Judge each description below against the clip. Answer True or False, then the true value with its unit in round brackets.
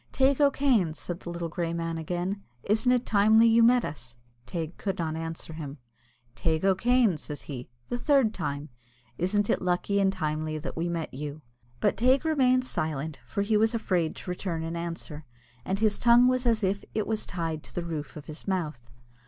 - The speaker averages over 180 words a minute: True (195 wpm)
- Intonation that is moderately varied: False (5.8 semitones)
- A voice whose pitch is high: False (180 Hz)